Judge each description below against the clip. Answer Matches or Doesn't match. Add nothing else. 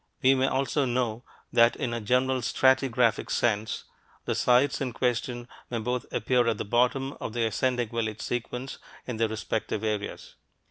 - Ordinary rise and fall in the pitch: Doesn't match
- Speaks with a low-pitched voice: Matches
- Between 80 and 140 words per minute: Doesn't match